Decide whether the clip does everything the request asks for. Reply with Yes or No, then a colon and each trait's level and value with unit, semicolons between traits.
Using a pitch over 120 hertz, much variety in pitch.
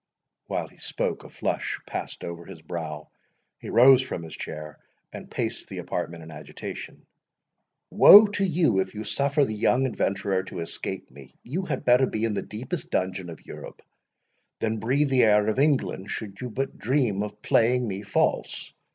No: low, 110 Hz; wide, 6.0 semitones